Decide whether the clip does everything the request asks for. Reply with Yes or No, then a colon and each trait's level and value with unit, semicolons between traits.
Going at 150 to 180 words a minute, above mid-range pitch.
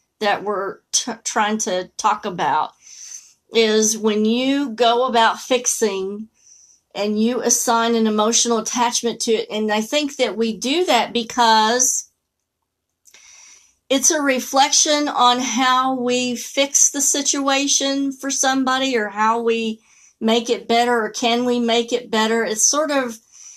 No: average, 140 wpm; high, 235 Hz